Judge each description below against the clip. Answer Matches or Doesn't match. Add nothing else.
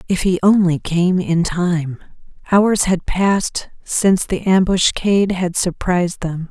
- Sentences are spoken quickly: Doesn't match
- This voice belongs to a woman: Matches